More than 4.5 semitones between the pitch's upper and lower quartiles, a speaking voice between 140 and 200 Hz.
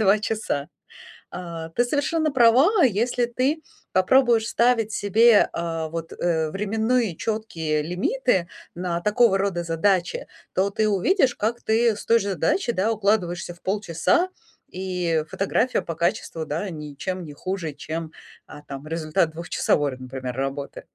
Yes: wide, 5.5 semitones; high, 190 Hz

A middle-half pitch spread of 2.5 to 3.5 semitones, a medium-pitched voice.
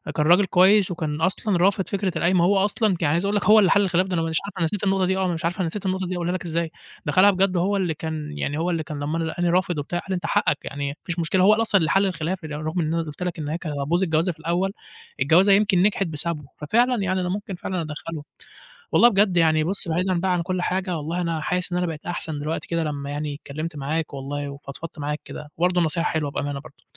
Yes: average, 3.2 semitones; medium, 170 Hz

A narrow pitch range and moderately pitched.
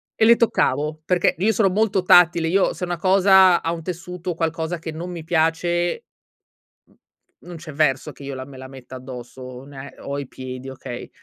No: average, 4.9 semitones; medium, 165 Hz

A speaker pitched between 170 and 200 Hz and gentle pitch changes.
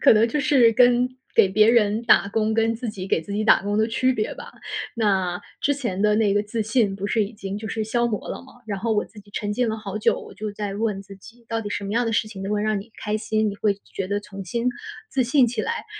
No: high, 215 Hz; narrow, 2.2 semitones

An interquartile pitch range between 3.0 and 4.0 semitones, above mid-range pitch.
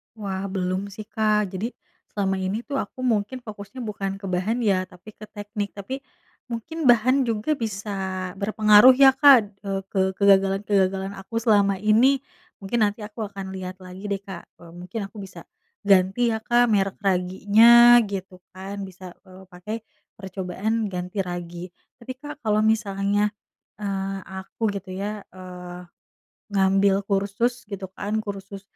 No: narrow, 2.4 semitones; high, 200 Hz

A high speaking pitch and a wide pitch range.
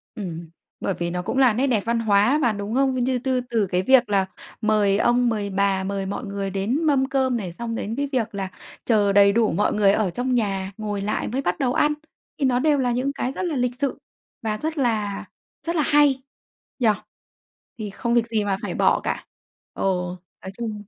No: high, 225 Hz; average, 4.4 semitones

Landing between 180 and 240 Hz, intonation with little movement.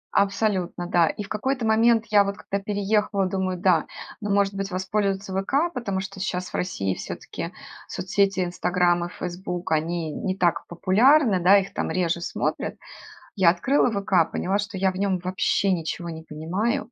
Yes: high, 190 Hz; narrow, 2.3 semitones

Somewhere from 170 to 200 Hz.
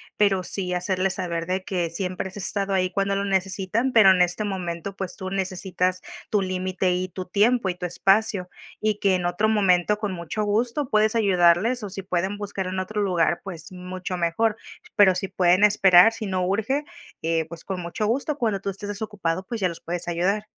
Yes: high, 190 Hz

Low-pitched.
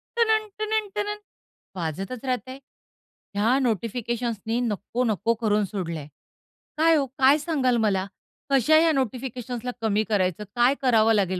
No: high, 240 Hz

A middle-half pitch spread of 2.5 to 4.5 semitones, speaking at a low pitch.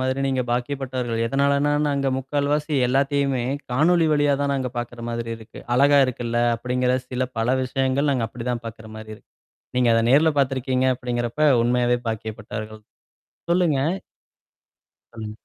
Yes: average, 2.9 semitones; low, 125 Hz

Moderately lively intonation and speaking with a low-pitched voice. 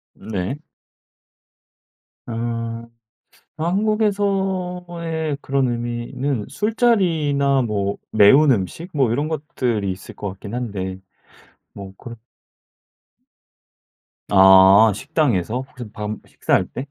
No: wide, 7.3 semitones; low, 125 Hz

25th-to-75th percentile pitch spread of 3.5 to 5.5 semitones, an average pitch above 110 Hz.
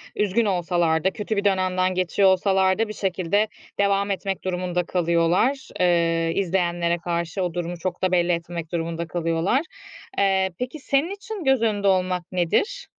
No: average, 2.7 semitones; medium, 185 Hz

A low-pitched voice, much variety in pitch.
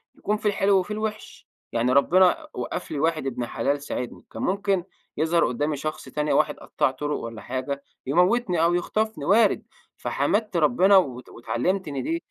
No: medium, 165 Hz; wide, 6.1 semitones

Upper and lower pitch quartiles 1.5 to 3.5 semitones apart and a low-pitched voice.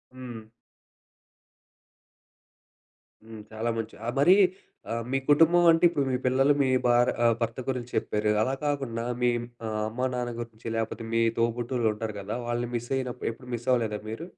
Yes: narrow, 2.4 semitones; low, 120 Hz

